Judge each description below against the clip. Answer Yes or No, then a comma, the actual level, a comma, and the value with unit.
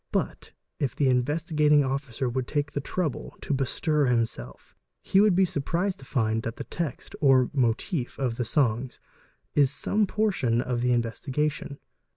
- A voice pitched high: No, low, 135 Hz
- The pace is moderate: Yes, average, 170 wpm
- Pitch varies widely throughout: No, average, 3.6 semitones